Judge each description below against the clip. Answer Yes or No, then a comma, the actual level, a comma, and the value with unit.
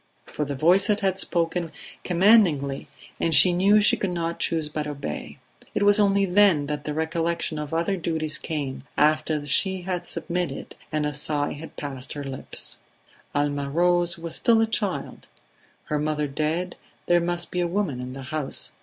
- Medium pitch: Yes, medium, 165 Hz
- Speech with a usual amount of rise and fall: Yes, average, 3.4 semitones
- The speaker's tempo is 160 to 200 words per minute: Yes, average, 170 wpm